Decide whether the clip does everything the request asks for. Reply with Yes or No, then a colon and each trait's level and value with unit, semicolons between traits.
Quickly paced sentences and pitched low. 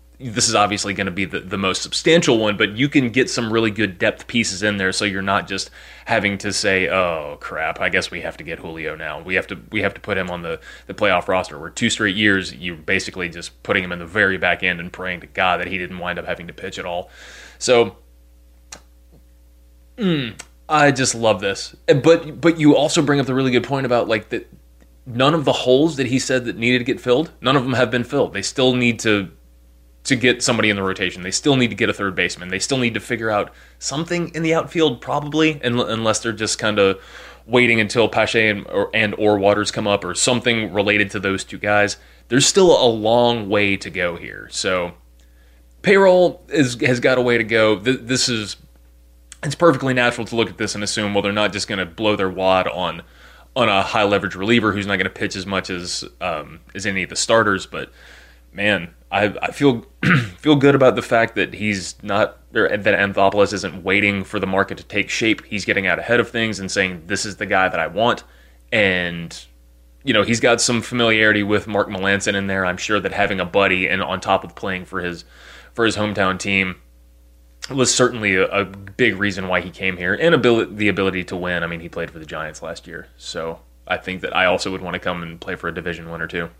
Yes: fast, 235 wpm; low, 100 Hz